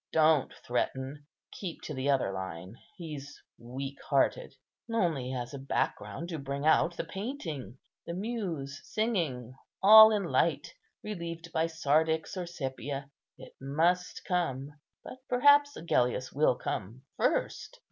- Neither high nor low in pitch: Yes, medium, 155 Hz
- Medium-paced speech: No, slow, 130 wpm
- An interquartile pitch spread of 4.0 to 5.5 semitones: Yes, average, 4.8 semitones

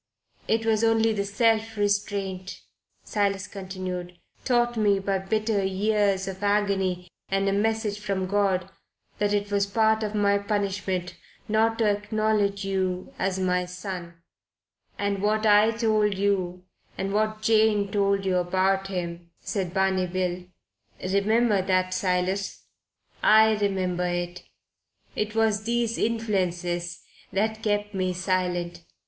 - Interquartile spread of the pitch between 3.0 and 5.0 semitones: No, narrow, 2.5 semitones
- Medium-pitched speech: No, high, 200 Hz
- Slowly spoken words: Yes, slow, 130 wpm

